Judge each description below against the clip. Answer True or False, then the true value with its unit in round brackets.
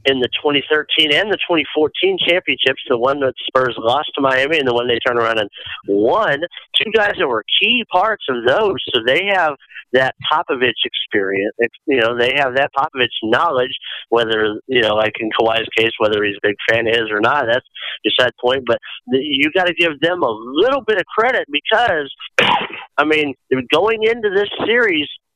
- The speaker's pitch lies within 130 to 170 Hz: True (135 Hz)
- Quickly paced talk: False (195 wpm)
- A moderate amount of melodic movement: False (6.8 semitones)